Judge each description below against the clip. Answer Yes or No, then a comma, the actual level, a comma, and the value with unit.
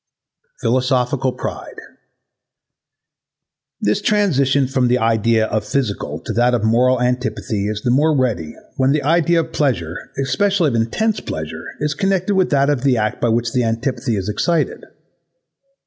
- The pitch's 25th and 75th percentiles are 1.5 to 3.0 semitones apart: No, average, 4.4 semitones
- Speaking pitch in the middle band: No, low, 130 Hz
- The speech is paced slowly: No, average, 150 wpm